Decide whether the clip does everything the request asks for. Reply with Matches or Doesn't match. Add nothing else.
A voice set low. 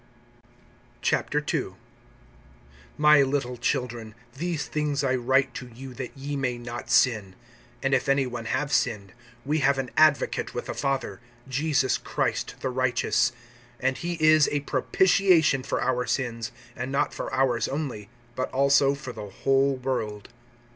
Matches